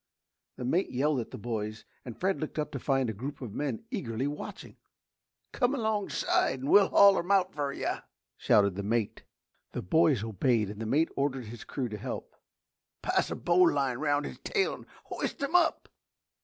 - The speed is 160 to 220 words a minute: Yes, average, 185 wpm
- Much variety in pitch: Yes, wide, 7.1 semitones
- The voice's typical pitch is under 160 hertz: Yes, medium, 140 Hz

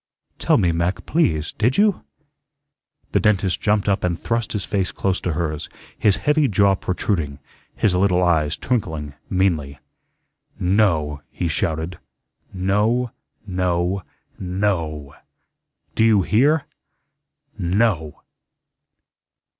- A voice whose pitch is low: Yes, very low, 95 Hz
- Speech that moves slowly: Yes, slow, 110 wpm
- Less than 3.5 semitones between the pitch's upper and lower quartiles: No, average, 4.2 semitones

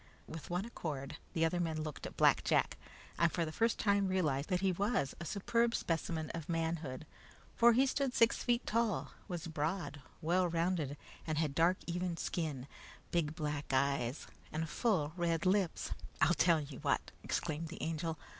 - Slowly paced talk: No, average, 175 wpm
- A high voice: No, medium, 165 Hz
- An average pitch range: Yes, average, 3.2 semitones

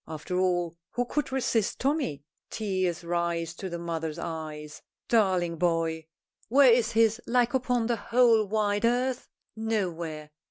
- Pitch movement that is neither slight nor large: No, wide, 5.8 semitones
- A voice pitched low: No, high, 190 Hz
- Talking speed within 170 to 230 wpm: No, slow, 135 wpm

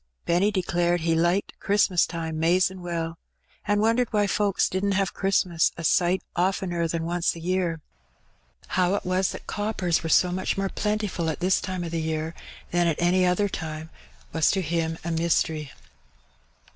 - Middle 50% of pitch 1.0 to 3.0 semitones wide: Yes, narrow, 2.5 semitones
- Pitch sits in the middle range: Yes, medium, 175 Hz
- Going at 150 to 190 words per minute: Yes, average, 185 wpm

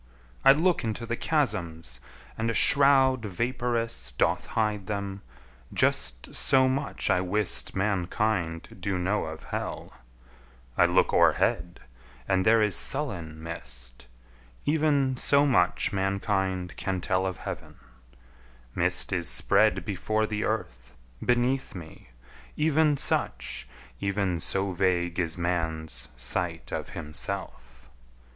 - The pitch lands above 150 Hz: No, very low, 95 Hz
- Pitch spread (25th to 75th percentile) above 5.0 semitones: Yes, wide, 5.6 semitones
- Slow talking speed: Yes, slow, 120 wpm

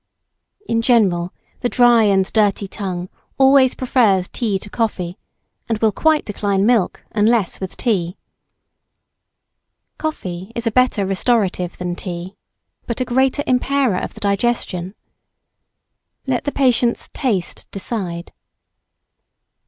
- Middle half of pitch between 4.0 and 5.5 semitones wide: Yes, average, 4.5 semitones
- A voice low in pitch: No, high, 215 Hz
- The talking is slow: Yes, slow, 120 wpm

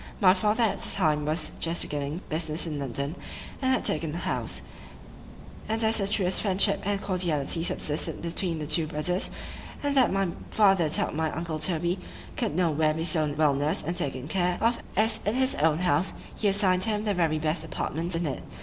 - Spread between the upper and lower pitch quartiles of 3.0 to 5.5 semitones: Yes, average, 4.1 semitones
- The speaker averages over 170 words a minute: Yes, average, 185 wpm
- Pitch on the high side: No, medium, 170 Hz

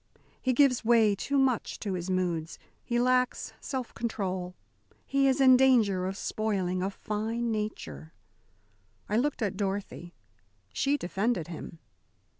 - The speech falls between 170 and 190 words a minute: No, slow, 135 wpm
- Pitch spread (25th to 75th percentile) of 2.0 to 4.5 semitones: No, average, 5.3 semitones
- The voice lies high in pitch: Yes, high, 215 Hz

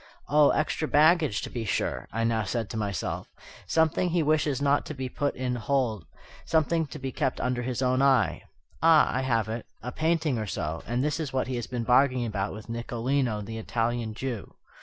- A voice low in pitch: Yes, low, 125 Hz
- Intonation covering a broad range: No, average, 4.2 semitones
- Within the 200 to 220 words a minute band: Yes, fast, 205 wpm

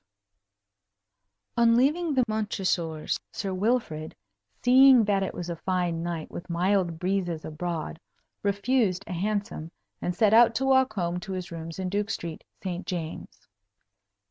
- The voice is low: No, high, 190 Hz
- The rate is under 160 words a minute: Yes, average, 145 wpm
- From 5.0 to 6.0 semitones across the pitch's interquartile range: No, average, 4.2 semitones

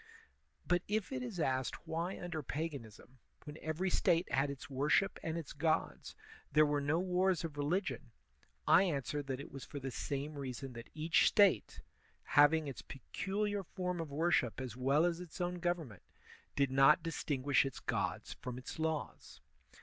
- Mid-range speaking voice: Yes, medium, 155 Hz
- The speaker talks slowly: No, average, 165 wpm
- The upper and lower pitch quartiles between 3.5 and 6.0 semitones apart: Yes, average, 4.4 semitones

